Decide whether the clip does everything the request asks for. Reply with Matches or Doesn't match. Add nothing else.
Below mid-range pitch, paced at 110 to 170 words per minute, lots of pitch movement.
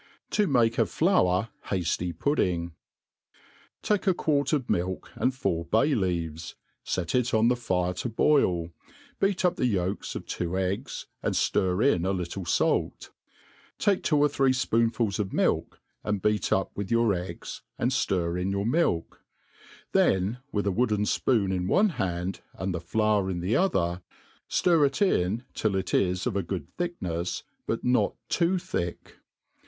Matches